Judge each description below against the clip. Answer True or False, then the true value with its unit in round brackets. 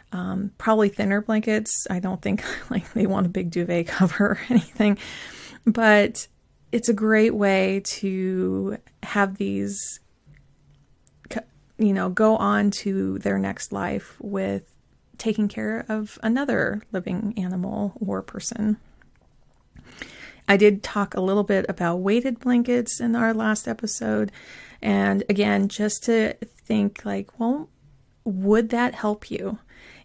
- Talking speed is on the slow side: True (130 wpm)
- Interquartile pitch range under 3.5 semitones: True (2.8 semitones)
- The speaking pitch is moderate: False (205 Hz)